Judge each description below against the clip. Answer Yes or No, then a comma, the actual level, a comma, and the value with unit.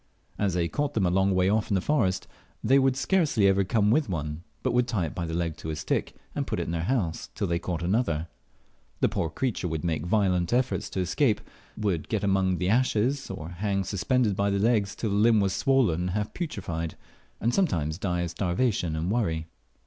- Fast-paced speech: Yes, fast, 220 wpm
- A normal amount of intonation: Yes, average, 4.9 semitones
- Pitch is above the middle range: No, very low, 95 Hz